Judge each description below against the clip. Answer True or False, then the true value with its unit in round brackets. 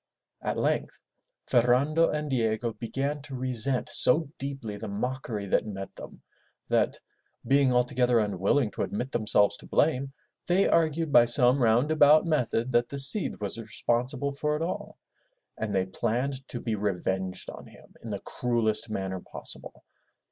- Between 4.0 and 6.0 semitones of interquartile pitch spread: True (4.4 semitones)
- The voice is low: True (125 Hz)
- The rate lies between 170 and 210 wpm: False (155 wpm)